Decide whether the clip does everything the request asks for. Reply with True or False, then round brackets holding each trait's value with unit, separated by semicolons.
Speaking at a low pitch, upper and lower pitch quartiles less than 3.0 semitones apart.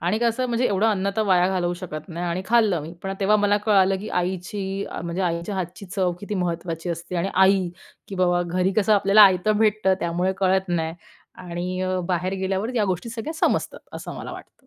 False (190 Hz; 2.6 semitones)